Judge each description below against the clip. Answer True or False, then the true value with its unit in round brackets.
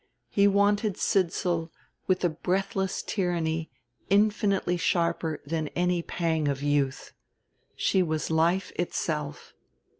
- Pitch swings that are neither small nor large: True (3.3 semitones)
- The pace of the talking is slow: True (110 wpm)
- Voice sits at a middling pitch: True (175 Hz)